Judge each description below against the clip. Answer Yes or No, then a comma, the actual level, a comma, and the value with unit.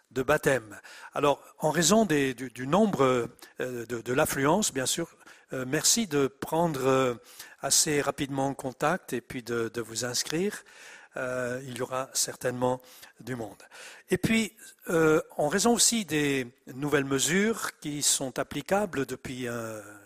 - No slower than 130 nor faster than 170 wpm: Yes, average, 155 wpm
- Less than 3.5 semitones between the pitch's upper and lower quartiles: No, average, 4.3 semitones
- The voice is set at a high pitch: No, low, 135 Hz